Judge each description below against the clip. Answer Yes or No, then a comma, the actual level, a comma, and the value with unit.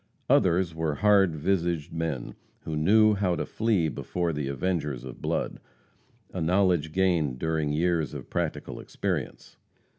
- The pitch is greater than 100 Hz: No, very low, 85 Hz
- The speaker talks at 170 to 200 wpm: No, average, 140 wpm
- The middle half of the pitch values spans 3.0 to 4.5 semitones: Yes, average, 3.5 semitones